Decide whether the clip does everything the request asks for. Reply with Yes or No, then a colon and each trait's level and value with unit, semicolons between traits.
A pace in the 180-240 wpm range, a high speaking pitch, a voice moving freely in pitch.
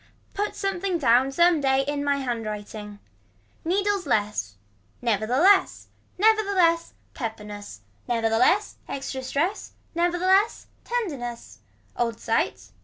No: slow, 135 wpm; very high, 275 Hz; wide, 8.5 semitones